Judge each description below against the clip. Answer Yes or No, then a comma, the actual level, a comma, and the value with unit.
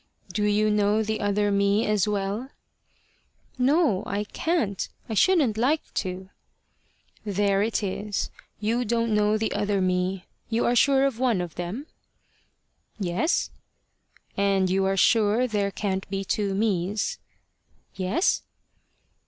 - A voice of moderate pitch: No, high, 210 Hz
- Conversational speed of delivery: No, slow, 130 wpm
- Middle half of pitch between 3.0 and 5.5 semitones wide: No, narrow, 2.6 semitones